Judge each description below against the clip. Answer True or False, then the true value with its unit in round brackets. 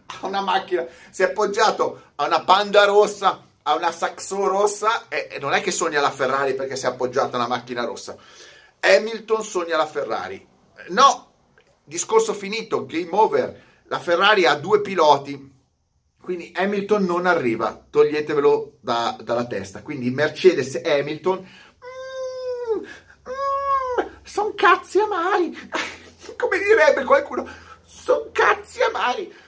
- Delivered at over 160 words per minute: False (135 wpm)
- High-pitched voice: True (205 Hz)